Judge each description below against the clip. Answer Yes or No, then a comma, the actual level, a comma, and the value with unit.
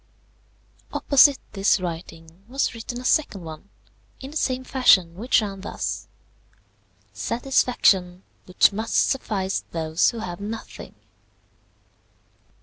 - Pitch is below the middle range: No, high, 200 Hz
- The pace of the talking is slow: Yes, slow, 110 wpm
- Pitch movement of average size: No, wide, 5.8 semitones